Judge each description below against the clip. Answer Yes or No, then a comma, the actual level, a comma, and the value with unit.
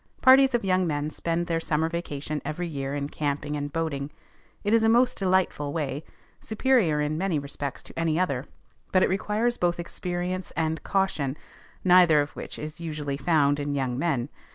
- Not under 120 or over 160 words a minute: No, average, 175 wpm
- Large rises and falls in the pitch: No, average, 4.1 semitones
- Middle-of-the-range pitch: Yes, medium, 160 Hz